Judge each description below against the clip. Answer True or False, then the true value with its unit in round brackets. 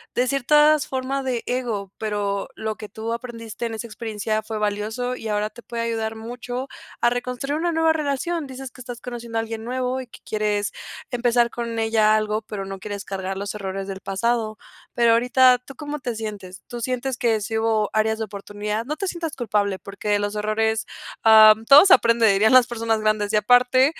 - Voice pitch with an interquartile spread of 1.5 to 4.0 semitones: True (2.8 semitones)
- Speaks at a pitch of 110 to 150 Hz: False (225 Hz)